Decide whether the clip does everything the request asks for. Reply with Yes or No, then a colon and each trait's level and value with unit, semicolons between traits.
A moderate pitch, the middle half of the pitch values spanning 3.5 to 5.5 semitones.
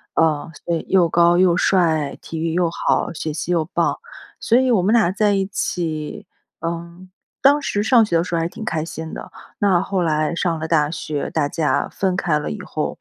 No: medium, 170 Hz; average, 3.1 semitones